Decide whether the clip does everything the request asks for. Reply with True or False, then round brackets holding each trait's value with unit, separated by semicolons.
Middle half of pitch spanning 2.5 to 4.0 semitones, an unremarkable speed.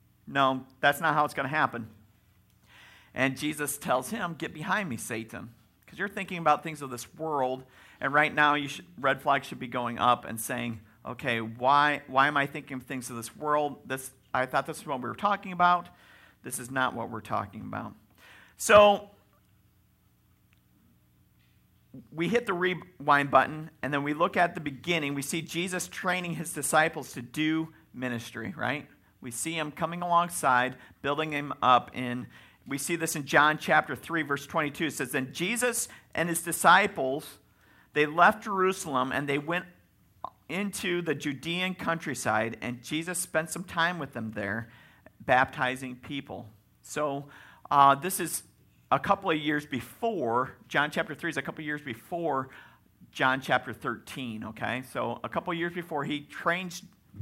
False (4.8 semitones; 170 wpm)